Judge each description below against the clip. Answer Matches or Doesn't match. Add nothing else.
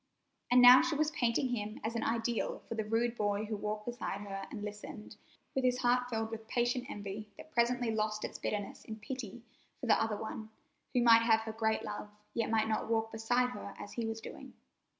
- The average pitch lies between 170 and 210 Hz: Doesn't match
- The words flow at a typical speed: Doesn't match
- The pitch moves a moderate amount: Doesn't match